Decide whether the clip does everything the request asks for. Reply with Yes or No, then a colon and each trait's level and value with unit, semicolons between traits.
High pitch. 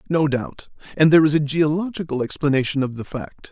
No: medium, 150 Hz